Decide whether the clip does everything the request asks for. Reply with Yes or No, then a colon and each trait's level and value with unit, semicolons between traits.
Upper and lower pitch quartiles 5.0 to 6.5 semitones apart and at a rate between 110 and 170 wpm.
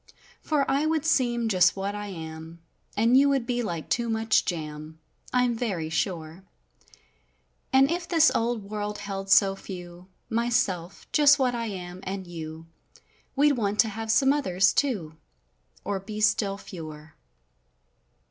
Yes: wide, 5.5 semitones; average, 150 wpm